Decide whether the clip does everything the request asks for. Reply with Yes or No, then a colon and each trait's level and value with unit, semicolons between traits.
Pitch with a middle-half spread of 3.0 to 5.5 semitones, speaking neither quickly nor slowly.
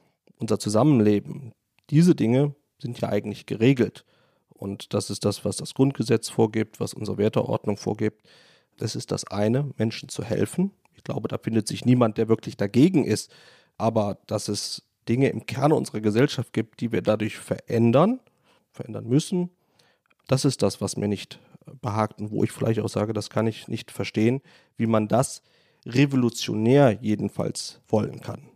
Yes: average, 4.1 semitones; average, 160 wpm